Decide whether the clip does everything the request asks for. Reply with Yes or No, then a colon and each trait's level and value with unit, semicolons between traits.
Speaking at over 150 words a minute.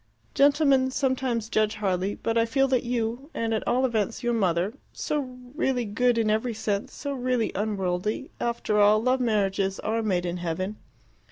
Yes: average, 170 wpm